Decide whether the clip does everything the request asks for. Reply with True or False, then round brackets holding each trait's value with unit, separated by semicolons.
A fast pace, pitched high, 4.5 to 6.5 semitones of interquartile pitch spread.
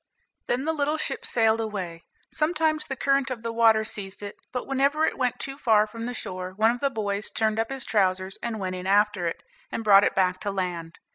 True (225 wpm; 220 Hz; 5.1 semitones)